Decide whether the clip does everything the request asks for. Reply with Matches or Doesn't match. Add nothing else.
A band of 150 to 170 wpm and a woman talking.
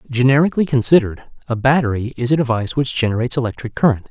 Doesn't match